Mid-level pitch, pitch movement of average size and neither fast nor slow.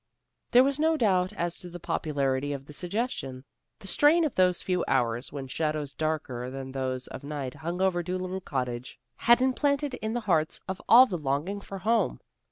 No: medium, 175 Hz; wide, 7.6 semitones; average, 185 wpm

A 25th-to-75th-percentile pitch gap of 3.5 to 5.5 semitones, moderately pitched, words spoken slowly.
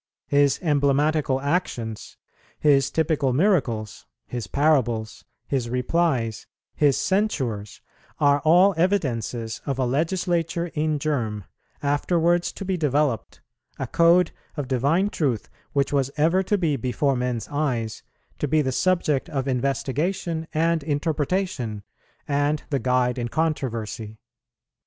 Yes: average, 4.5 semitones; medium, 145 Hz; slow, 120 wpm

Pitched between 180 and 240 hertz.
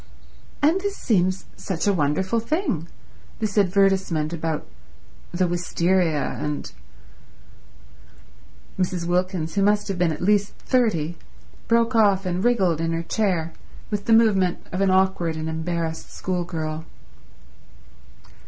Yes: medium, 185 Hz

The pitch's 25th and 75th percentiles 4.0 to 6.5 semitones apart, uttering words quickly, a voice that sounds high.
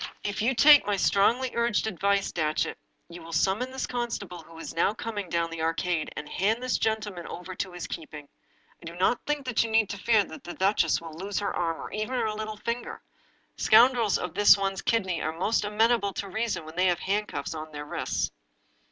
Yes: average, 4.7 semitones; fast, 215 wpm; high, 200 Hz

